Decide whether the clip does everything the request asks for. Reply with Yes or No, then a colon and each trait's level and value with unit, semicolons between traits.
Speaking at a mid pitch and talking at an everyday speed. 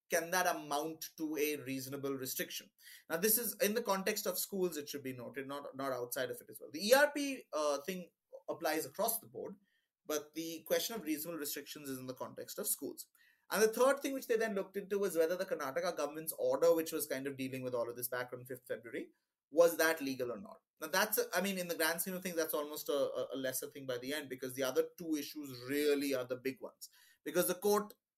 No: medium, 165 Hz; fast, 240 wpm